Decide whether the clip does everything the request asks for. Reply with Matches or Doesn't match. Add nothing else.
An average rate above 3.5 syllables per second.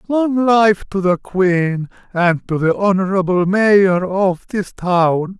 Doesn't match